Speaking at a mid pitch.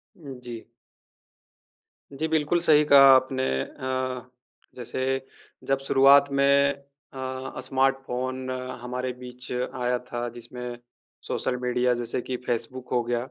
No: low, 130 Hz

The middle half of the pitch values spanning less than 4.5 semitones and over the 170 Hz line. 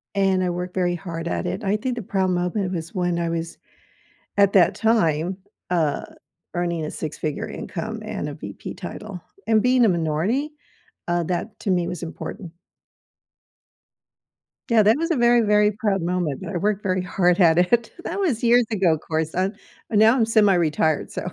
Yes: average, 3.9 semitones; medium, 185 Hz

